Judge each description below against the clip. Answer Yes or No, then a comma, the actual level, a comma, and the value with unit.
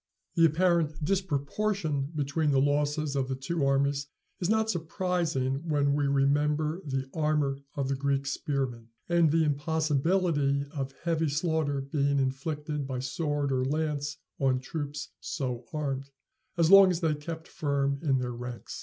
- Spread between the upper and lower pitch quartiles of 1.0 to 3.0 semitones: Yes, average, 2.7 semitones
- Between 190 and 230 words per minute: No, average, 150 wpm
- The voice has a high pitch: No, medium, 145 Hz